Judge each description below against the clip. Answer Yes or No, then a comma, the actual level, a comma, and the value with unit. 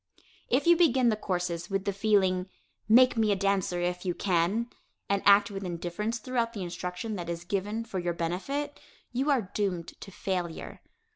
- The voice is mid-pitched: No, high, 195 Hz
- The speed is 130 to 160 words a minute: No, average, 180 wpm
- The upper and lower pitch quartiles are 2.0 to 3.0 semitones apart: No, average, 4.2 semitones